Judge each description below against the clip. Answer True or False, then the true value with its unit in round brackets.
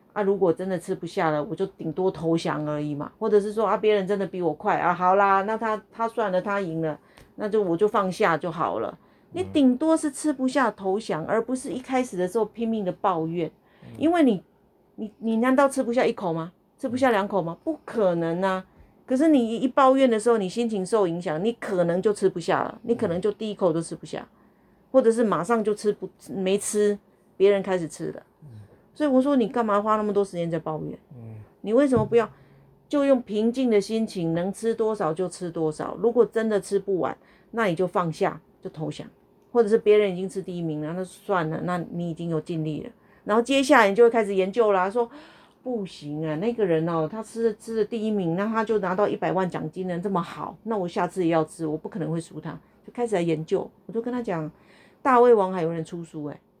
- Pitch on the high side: True (200 Hz)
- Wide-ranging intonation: False (4.5 semitones)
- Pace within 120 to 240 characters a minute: False (315 characters per minute)